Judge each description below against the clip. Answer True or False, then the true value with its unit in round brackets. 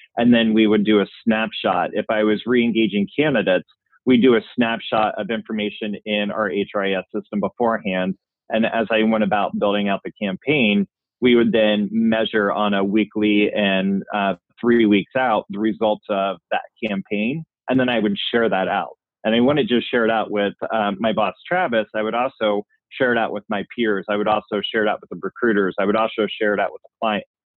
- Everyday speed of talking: False (210 wpm)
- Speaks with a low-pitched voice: True (105 Hz)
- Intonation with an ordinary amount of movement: False (1.6 semitones)